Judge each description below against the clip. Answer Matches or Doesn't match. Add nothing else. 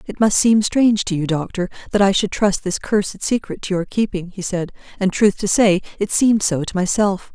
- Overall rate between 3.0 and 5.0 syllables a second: Doesn't match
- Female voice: Matches